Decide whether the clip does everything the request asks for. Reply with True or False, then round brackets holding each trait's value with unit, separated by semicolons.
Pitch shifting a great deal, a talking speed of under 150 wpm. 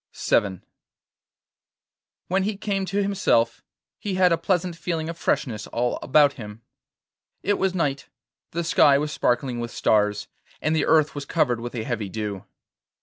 False (7.2 semitones; 155 wpm)